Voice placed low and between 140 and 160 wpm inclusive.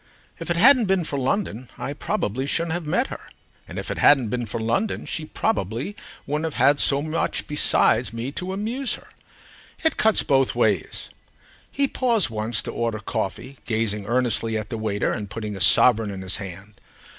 No: low, 125 Hz; average, 185 wpm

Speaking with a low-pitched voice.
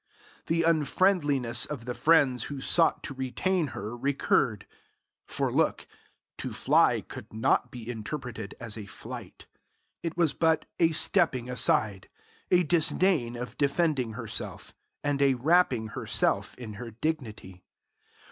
Yes: low, 130 Hz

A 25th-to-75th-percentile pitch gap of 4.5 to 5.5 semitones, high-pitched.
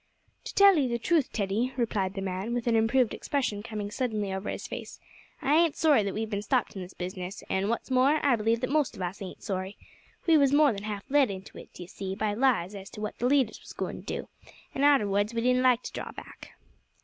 Yes: average, 4.8 semitones; high, 225 Hz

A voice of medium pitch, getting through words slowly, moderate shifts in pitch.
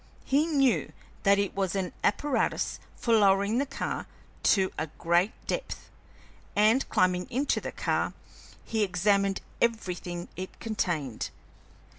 No: high, 200 Hz; slow, 125 wpm; average, 4.2 semitones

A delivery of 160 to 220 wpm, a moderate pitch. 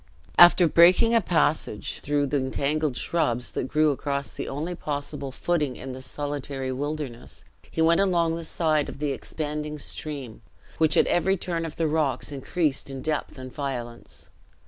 Yes: average, 165 wpm; medium, 150 Hz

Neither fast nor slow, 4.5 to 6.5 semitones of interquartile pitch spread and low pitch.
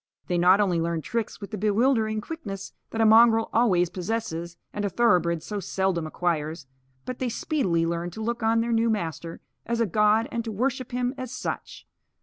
No: average, 190 wpm; average, 5.0 semitones; high, 210 Hz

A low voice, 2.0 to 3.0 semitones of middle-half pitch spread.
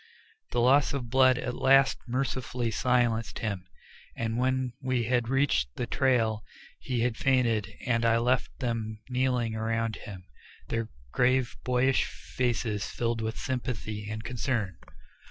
Yes: low, 120 Hz; narrow, 2.4 semitones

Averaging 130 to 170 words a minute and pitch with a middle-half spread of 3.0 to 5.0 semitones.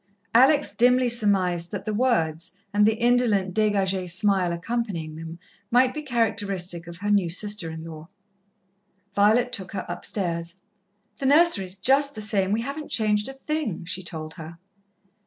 No: average, 155 wpm; wide, 5.5 semitones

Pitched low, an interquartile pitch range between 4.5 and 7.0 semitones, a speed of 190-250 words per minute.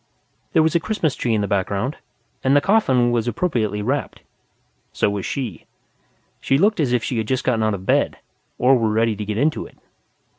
Yes: low, 120 Hz; average, 4.9 semitones; average, 200 wpm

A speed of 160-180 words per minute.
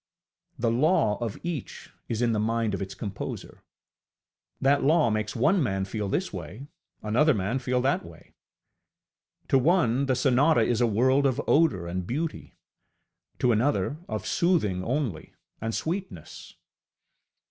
No: average, 145 wpm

